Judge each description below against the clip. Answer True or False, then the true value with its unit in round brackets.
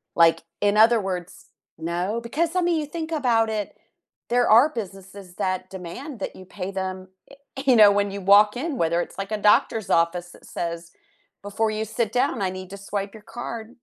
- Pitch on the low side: False (205 Hz)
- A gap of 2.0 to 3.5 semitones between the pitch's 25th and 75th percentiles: False (4.0 semitones)